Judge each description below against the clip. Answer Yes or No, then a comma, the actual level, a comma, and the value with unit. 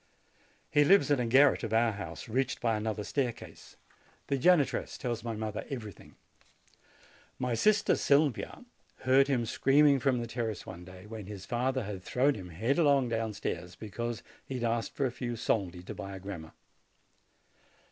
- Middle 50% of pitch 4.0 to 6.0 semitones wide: Yes, average, 4.3 semitones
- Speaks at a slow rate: No, average, 170 wpm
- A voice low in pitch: Yes, low, 120 Hz